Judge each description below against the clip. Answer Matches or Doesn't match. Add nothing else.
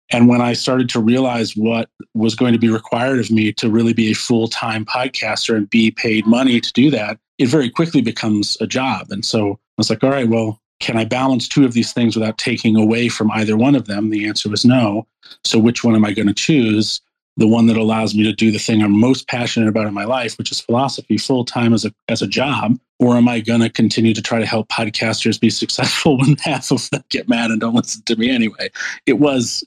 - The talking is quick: Matches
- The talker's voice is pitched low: Matches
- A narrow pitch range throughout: Matches